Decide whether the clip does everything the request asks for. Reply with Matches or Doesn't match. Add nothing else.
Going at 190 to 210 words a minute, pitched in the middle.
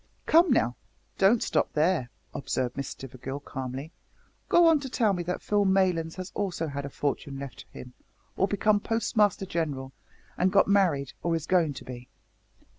Doesn't match